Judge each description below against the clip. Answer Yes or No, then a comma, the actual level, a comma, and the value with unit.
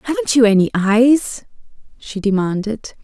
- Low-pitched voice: No, high, 220 Hz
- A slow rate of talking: Yes, slow, 120 wpm